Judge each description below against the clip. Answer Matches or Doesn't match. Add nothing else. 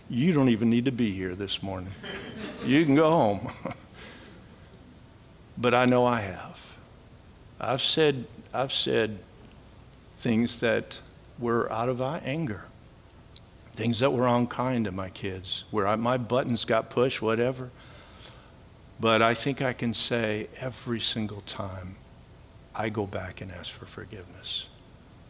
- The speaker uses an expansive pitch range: Doesn't match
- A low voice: Matches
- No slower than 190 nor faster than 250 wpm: Doesn't match